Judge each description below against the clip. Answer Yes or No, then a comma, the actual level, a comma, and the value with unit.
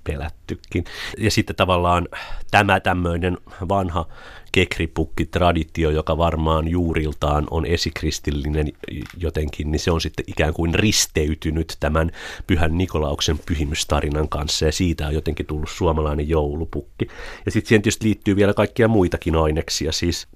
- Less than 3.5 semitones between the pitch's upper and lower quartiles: Yes, average, 2.9 semitones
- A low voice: Yes, very low, 80 Hz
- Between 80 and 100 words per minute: No, average, 125 wpm